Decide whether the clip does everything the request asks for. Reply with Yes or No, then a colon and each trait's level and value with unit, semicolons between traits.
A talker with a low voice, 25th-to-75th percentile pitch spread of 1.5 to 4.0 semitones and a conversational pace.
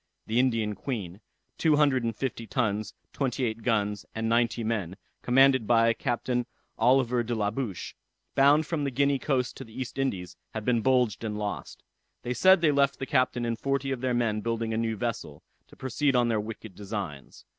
Yes: low, 120 Hz; average, 3.2 semitones; average, 190 wpm